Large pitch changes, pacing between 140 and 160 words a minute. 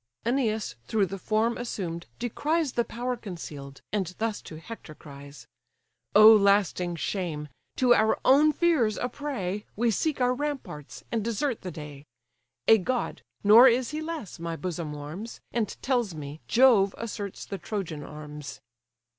Yes: wide, 6.5 semitones; average, 150 wpm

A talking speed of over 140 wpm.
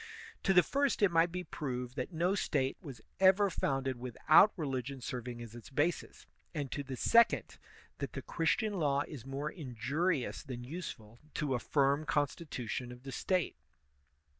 Yes: average, 165 wpm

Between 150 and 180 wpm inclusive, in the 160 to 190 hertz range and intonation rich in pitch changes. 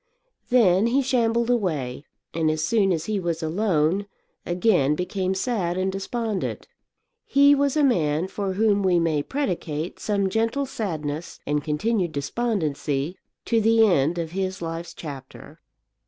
No: average, 140 wpm; medium, 185 Hz; wide, 6.0 semitones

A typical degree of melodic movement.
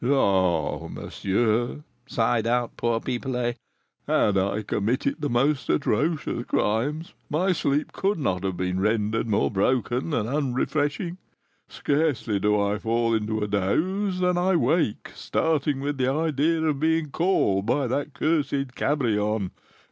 No: wide, 6.0 semitones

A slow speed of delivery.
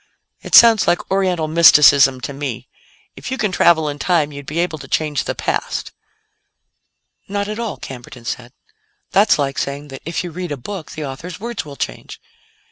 No: average, 185 wpm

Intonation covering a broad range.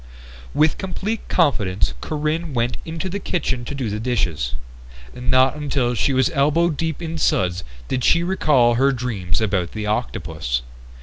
Yes: wide, 6.9 semitones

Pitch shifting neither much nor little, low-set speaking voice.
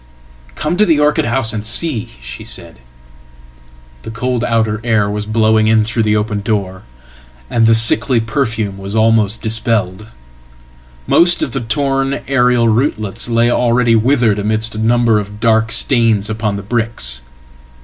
No: narrow, 2.3 semitones; low, 110 Hz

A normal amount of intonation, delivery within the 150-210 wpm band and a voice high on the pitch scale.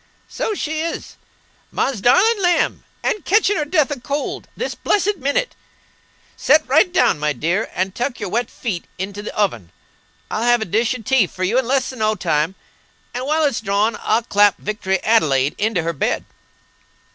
No: wide, 7.2 semitones; average, 180 wpm; high, 230 Hz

